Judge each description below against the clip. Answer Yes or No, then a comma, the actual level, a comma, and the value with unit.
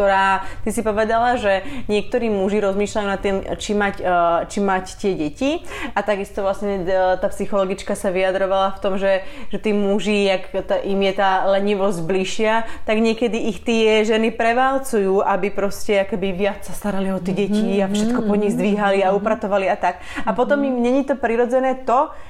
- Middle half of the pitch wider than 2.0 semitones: Yes, narrow, 2.6 semitones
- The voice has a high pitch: Yes, high, 205 Hz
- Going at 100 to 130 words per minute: No, fast, 165 wpm